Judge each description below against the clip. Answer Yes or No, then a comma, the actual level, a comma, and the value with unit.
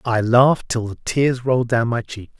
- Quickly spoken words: Yes, fast, 225 wpm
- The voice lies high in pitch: No, low, 120 Hz